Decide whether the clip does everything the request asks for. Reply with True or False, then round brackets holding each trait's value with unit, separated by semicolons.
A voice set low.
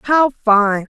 False (235 Hz)